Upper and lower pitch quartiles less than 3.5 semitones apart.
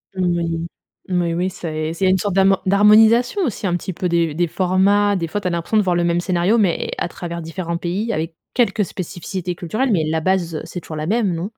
Yes: average, 2.9 semitones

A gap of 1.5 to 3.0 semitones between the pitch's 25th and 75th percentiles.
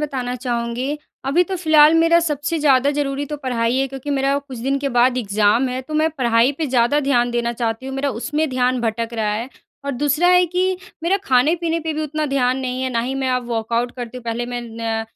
No: average, 3.5 semitones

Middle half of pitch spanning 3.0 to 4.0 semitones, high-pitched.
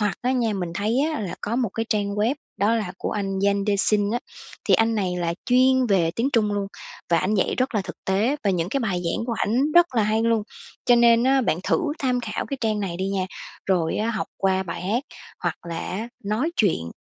Yes: average, 3.6 semitones; high, 210 Hz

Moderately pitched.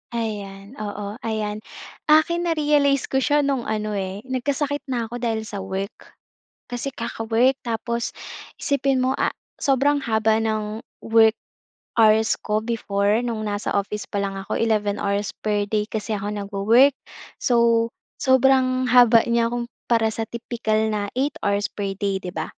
No: high, 225 Hz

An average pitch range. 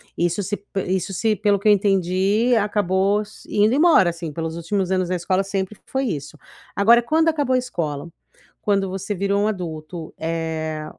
Yes: average, 3.6 semitones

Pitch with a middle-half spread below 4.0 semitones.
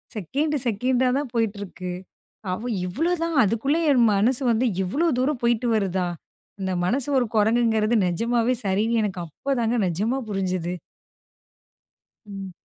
No: average, 4.6 semitones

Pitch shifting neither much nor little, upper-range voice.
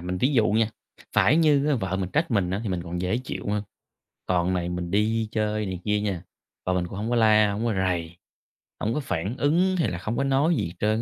No: average, 4.4 semitones; low, 105 Hz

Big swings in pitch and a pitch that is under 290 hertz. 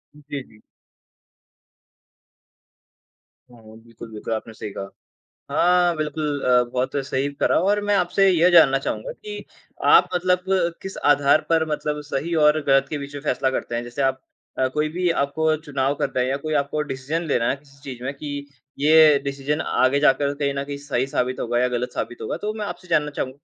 No: average, 2.9 semitones; medium, 140 Hz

